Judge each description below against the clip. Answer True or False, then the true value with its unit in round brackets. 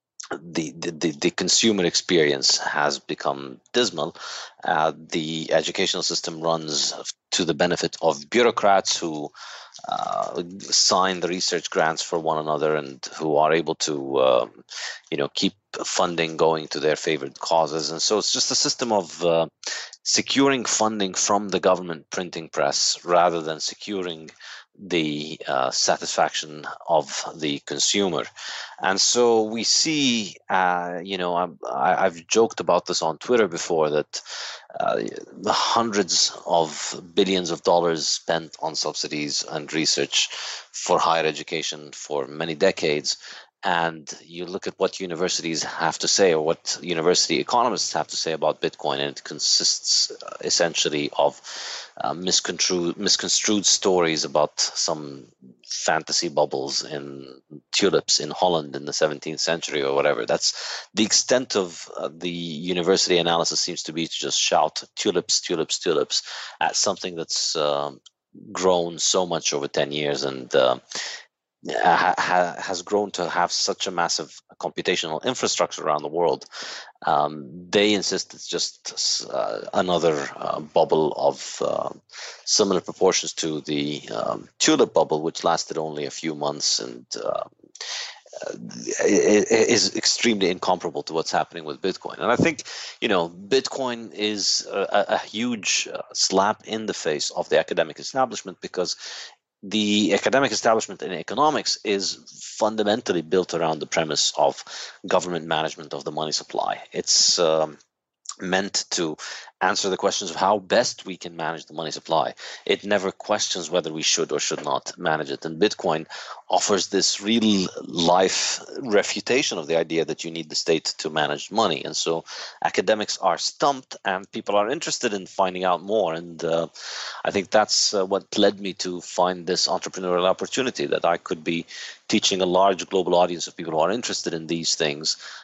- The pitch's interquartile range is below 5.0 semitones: True (3.8 semitones)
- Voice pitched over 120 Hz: False (85 Hz)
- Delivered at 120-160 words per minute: True (155 wpm)